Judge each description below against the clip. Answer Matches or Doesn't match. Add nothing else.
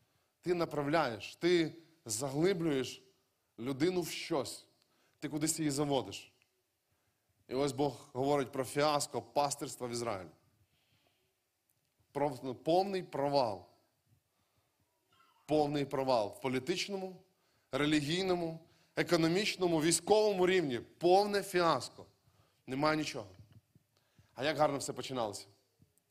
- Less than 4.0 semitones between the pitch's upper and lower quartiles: Doesn't match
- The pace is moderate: Doesn't match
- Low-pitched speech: Doesn't match